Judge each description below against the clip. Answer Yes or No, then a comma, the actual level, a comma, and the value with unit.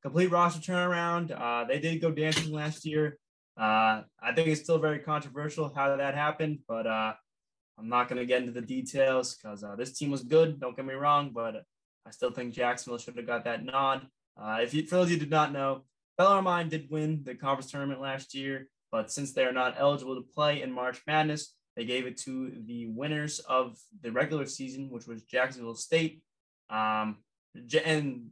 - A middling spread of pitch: Yes, average, 3.9 semitones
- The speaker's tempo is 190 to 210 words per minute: Yes, average, 200 wpm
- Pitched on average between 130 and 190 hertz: Yes, low, 135 Hz